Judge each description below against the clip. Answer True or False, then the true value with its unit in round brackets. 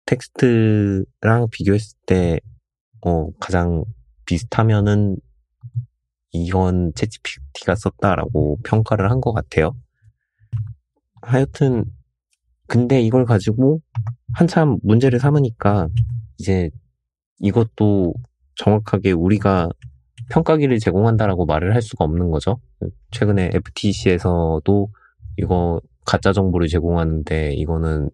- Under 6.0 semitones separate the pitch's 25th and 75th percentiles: True (5.3 semitones)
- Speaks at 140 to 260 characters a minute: True (235 characters per minute)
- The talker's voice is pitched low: True (100 Hz)